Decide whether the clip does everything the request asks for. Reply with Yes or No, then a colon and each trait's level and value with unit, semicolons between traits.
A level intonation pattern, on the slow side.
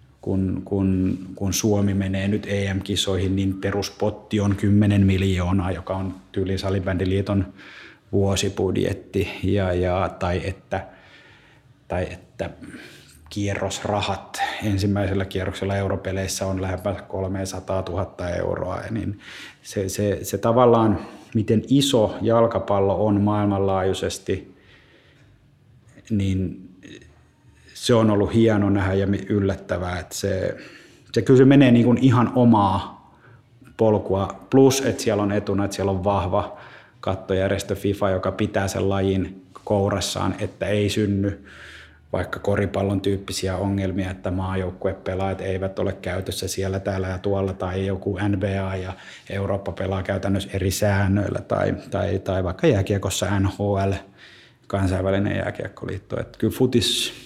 No: narrow, 1.4 semitones; average, 115 wpm